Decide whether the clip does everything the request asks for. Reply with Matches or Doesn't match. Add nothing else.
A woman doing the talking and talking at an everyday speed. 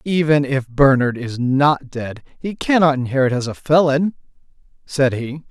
Doesn't match